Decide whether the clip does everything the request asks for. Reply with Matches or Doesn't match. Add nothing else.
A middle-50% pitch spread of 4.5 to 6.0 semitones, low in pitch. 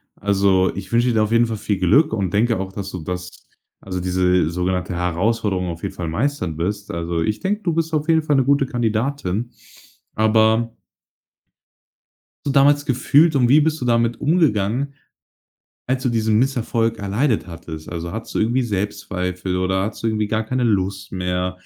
Matches